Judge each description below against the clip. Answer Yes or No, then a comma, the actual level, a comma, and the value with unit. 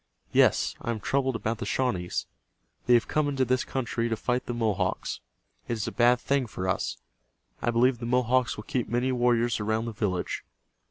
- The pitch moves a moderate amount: No, narrow, 2.3 semitones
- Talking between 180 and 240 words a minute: Yes, average, 195 wpm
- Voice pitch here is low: Yes, low, 120 Hz